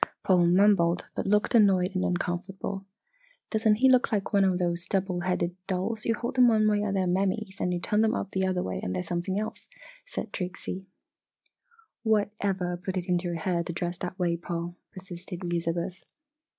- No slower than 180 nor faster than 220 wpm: Yes, average, 200 wpm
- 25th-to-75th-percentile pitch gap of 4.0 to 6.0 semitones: No, average, 2.8 semitones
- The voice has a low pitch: No, medium, 185 Hz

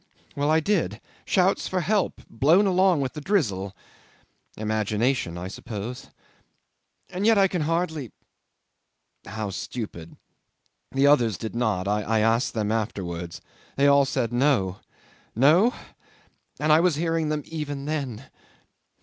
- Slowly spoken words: Yes, slow, 130 wpm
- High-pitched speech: No, low, 135 Hz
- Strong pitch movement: Yes, wide, 6.9 semitones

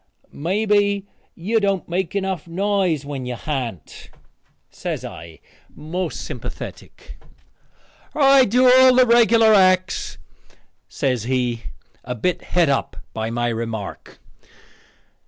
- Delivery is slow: Yes, slow, 110 wpm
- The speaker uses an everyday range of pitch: No, wide, 8.5 semitones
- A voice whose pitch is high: No, medium, 180 Hz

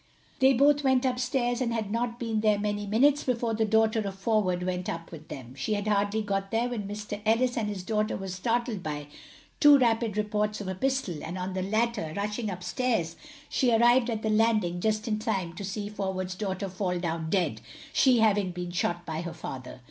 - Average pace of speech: No, fast, 210 wpm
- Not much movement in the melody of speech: No, average, 4.0 semitones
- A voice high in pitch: Yes, high, 210 Hz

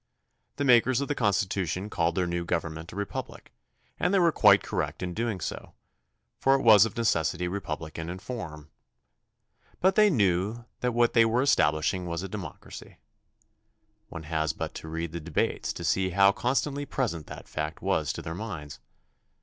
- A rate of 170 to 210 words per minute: Yes, average, 175 wpm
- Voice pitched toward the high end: No, very low, 95 Hz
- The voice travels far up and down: Yes, wide, 6.0 semitones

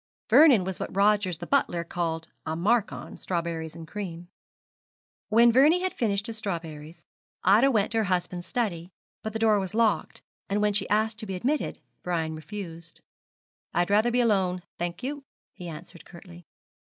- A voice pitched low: No, high, 195 Hz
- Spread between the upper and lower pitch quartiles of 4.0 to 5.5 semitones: Yes, average, 4.4 semitones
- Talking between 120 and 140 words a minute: No, average, 170 wpm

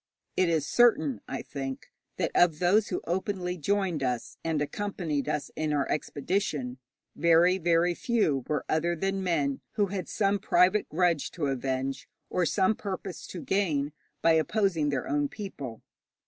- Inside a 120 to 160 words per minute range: Yes, average, 155 wpm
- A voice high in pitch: No, medium, 170 Hz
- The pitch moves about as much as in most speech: Yes, average, 4.7 semitones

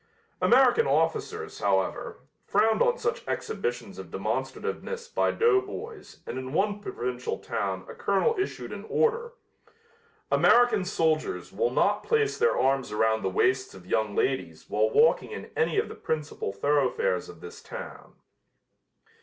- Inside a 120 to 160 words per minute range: Yes, average, 140 wpm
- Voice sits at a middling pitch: No, high, 225 Hz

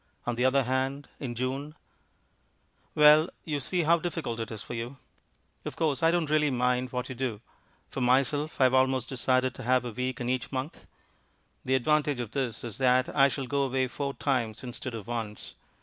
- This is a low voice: Yes, low, 130 Hz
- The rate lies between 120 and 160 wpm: No, average, 195 wpm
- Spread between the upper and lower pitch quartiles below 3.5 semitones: Yes, narrow, 2.5 semitones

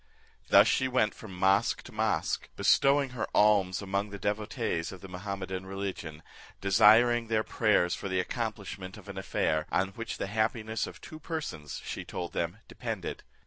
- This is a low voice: Yes, low, 100 Hz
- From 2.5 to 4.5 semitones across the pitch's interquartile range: Yes, average, 3.0 semitones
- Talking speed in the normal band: Yes, average, 165 wpm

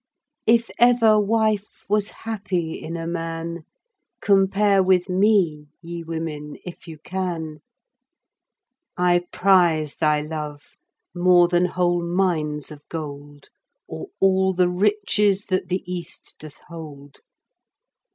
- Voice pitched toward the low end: No, medium, 175 Hz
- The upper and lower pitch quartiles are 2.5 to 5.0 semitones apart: Yes, average, 3.4 semitones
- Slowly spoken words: Yes, slow, 115 wpm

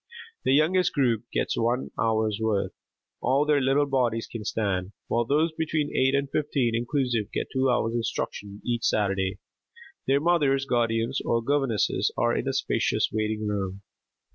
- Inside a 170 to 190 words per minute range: No, average, 155 wpm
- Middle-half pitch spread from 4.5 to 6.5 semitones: No, average, 4.1 semitones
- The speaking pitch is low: Yes, low, 120 Hz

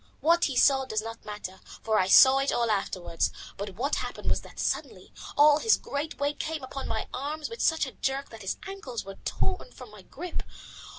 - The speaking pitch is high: Yes, very high, 265 Hz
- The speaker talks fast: Yes, fast, 210 wpm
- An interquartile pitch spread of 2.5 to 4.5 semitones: No, wide, 5.5 semitones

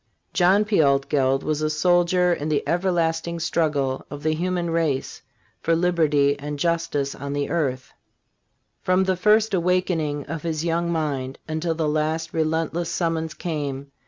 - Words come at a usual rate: Yes, average, 150 wpm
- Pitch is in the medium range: Yes, medium, 160 Hz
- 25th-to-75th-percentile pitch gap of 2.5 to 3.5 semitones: Yes, average, 2.8 semitones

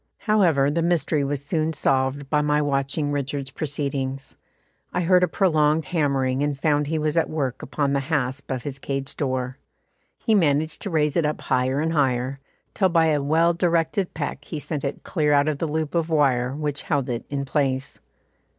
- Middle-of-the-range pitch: Yes, medium, 145 Hz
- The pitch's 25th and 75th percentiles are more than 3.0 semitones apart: No, narrow, 2.6 semitones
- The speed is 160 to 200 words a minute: Yes, average, 195 wpm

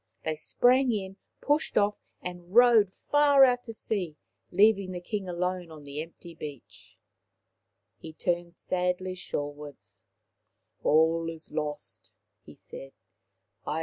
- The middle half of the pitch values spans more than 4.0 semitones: Yes, average, 5.0 semitones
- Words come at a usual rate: No, slow, 125 wpm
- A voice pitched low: No, medium, 180 Hz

